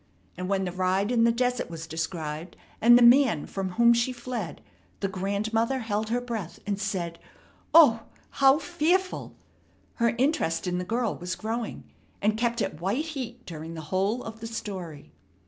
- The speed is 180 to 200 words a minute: No, average, 170 wpm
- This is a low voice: No, high, 220 Hz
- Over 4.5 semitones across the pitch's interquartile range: Yes, average, 4.9 semitones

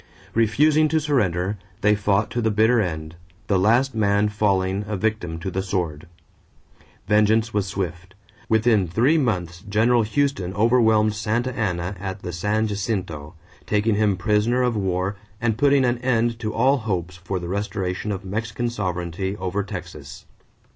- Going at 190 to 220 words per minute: No, average, 155 wpm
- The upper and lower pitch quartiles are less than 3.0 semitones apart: No, average, 3.4 semitones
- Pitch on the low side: Yes, low, 105 Hz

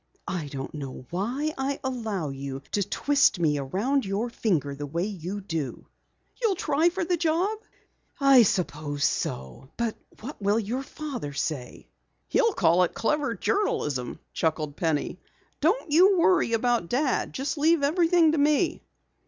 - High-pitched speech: Yes, high, 230 Hz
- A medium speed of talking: Yes, average, 150 wpm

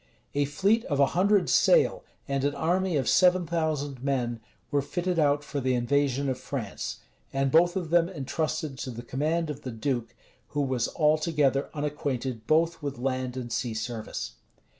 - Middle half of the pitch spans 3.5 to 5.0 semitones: Yes, average, 3.8 semitones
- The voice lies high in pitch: No, medium, 145 Hz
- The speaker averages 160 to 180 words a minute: Yes, average, 170 wpm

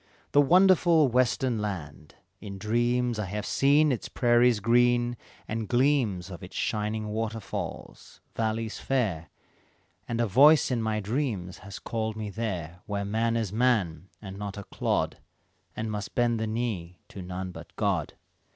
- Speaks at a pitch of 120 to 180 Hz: No, low, 110 Hz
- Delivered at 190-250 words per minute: No, average, 155 wpm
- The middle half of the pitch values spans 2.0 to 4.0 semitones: Yes, average, 3.3 semitones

